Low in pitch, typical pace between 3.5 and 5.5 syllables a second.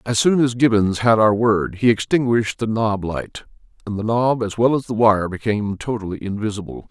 Yes: low, 110 Hz; 5.3 syllables/s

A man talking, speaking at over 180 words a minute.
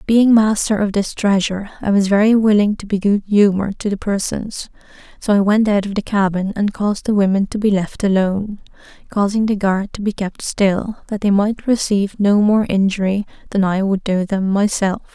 No: female; average, 200 wpm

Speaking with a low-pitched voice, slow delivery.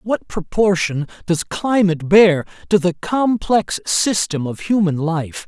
No: medium, 185 Hz; slow, 130 wpm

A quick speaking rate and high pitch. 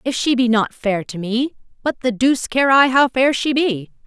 Yes: fast, 235 wpm; high, 245 Hz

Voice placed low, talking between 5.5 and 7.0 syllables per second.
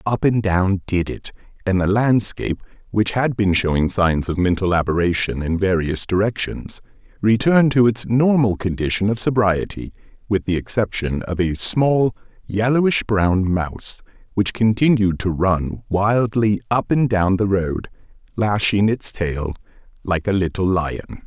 No: low, 100 Hz; 4.5 syllables/s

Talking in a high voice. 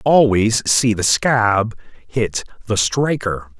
No: low, 115 Hz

